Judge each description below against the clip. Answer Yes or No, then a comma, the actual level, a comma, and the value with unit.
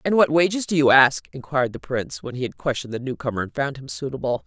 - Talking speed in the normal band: No, fast, 270 wpm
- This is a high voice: No, medium, 145 Hz